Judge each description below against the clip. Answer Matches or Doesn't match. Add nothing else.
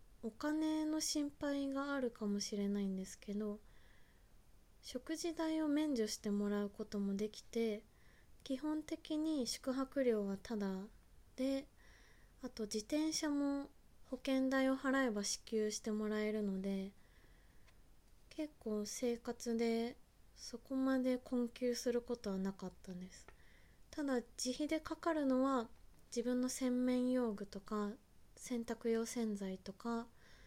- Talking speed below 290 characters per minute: Matches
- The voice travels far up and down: Doesn't match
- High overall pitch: Matches